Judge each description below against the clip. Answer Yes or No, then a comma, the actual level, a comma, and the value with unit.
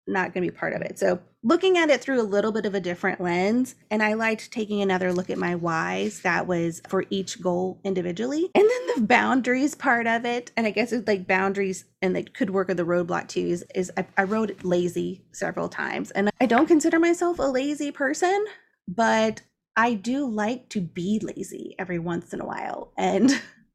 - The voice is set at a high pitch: Yes, high, 215 Hz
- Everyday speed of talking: No, fast, 215 wpm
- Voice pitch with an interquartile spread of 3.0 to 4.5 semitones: No, average, 5.1 semitones